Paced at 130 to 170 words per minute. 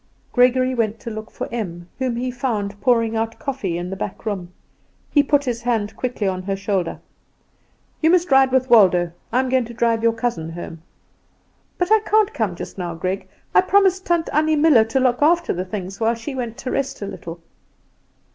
No: average, 200 wpm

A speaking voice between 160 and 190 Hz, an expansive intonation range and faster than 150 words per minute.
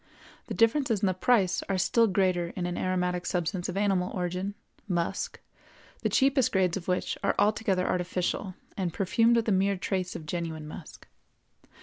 No: medium, 185 Hz; narrow, 2.4 semitones; average, 165 wpm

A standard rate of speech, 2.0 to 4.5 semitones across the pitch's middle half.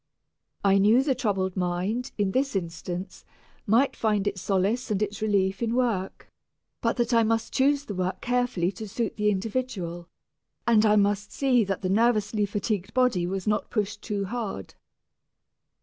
Yes: average, 165 wpm; average, 3.5 semitones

